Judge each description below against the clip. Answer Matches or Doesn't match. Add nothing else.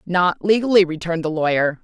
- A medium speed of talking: Matches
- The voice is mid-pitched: Matches